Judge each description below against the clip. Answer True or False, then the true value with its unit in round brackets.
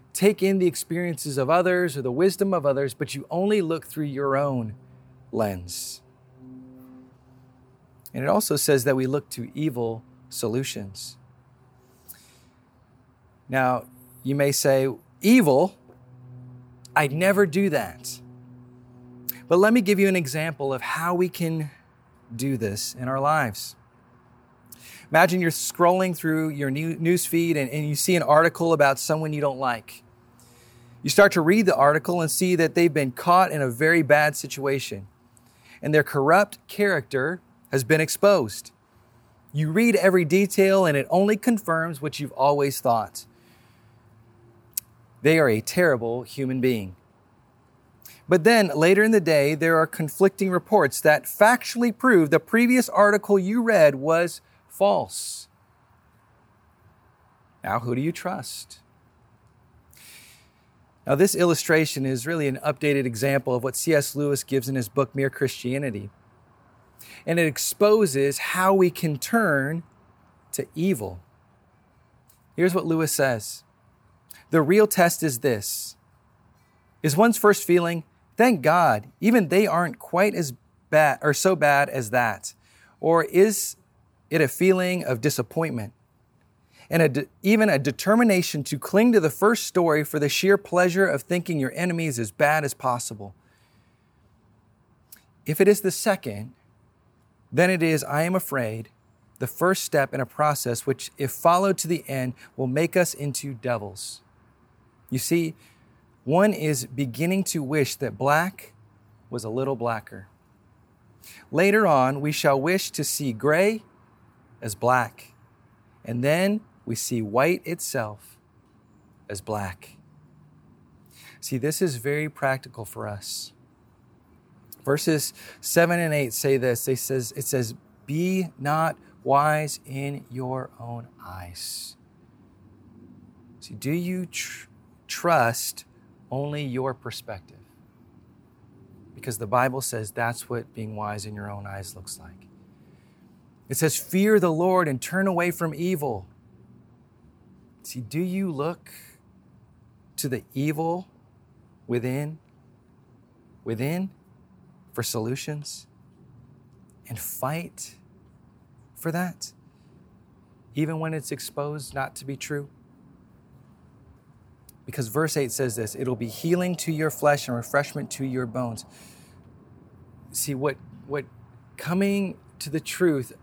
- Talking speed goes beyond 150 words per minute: False (135 wpm)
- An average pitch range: False (5.8 semitones)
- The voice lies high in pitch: False (135 Hz)